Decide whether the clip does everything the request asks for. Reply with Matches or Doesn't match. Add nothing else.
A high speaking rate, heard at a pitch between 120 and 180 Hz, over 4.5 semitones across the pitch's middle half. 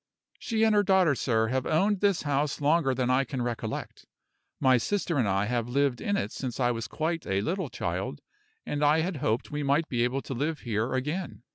Matches